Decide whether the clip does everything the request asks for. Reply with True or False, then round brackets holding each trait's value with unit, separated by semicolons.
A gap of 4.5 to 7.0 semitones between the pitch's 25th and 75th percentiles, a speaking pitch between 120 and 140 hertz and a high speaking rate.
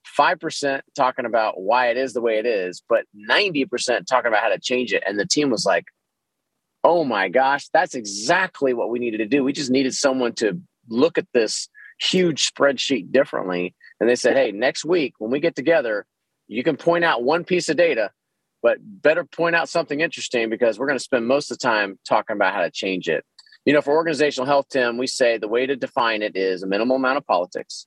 True (5.1 semitones; 135 Hz; 220 wpm)